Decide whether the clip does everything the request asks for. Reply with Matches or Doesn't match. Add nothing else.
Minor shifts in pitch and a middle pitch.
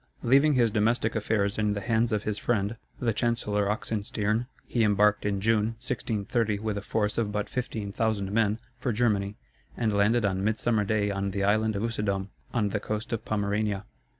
Doesn't match